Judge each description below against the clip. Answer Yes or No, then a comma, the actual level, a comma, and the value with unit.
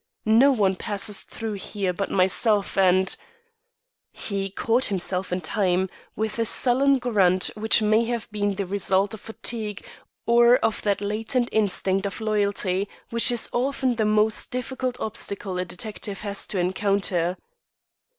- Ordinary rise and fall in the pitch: Yes, average, 3.0 semitones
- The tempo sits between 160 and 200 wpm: No, average, 150 wpm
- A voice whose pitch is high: Yes, high, 210 Hz